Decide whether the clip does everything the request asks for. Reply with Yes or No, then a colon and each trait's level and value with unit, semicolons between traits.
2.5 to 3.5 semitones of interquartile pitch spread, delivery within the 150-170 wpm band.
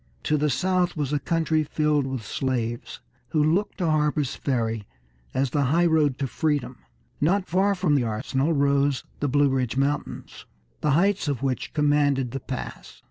Yes: average, 3.0 semitones; average, 165 wpm